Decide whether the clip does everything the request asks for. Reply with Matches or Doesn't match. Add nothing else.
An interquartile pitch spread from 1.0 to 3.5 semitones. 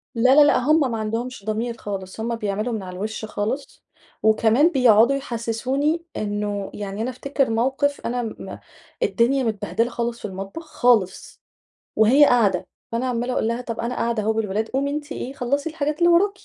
Doesn't match